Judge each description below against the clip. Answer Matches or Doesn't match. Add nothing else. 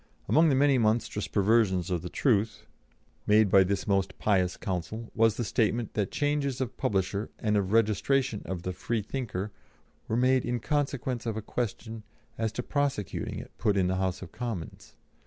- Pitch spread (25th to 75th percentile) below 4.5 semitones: Matches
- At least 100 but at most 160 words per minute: Doesn't match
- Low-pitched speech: Matches